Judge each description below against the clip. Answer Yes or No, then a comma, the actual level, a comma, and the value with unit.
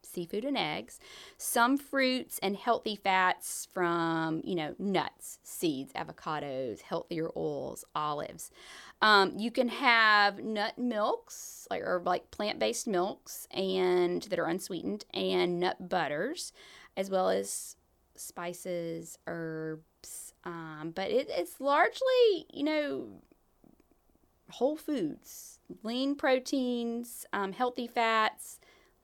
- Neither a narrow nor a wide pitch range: No, wide, 6.6 semitones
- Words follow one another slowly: Yes, slow, 110 wpm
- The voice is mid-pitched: No, high, 200 Hz